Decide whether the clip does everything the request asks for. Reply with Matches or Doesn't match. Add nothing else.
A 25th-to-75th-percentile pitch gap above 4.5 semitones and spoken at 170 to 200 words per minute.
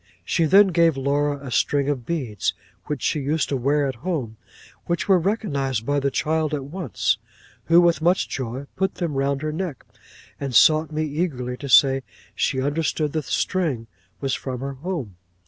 Doesn't match